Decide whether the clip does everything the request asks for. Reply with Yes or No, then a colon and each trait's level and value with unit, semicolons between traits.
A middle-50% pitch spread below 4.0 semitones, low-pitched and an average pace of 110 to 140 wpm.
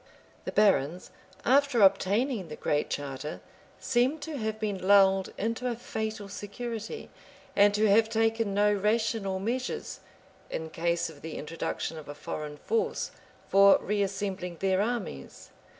No: average, 3.6 semitones; high, 205 Hz; slow, 135 wpm